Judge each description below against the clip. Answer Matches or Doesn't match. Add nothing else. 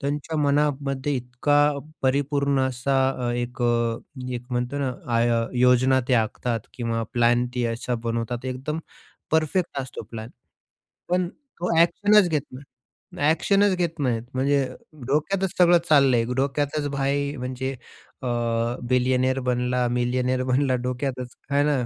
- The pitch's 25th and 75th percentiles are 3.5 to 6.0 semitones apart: Doesn't match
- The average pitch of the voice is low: Matches